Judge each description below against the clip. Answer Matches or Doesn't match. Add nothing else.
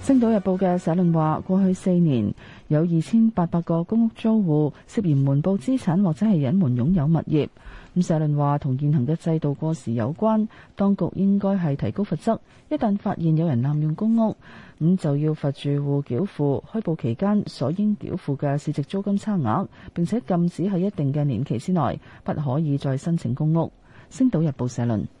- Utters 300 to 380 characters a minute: Doesn't match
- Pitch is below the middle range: Doesn't match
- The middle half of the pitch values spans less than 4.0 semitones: Doesn't match